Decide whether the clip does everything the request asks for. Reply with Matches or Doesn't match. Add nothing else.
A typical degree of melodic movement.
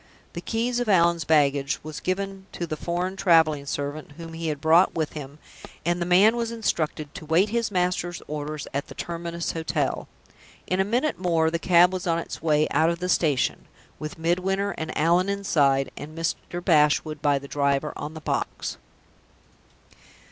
Matches